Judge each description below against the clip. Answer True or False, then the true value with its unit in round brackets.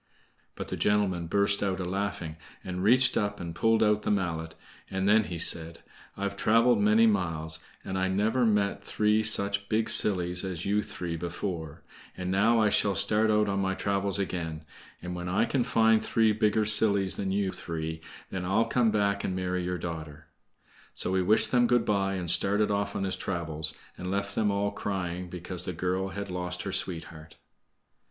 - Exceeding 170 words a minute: True (190 wpm)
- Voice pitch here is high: False (95 Hz)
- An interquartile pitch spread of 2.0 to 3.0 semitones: True (2.7 semitones)